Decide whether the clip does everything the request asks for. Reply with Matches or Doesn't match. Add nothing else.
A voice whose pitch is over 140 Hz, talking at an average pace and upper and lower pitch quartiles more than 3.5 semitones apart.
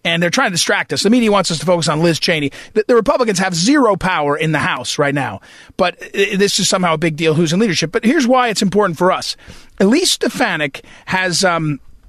Doesn't match